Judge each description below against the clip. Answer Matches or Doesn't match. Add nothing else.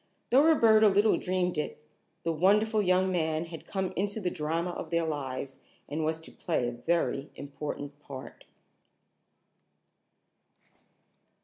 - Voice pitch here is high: Doesn't match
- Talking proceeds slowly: Matches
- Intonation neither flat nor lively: Matches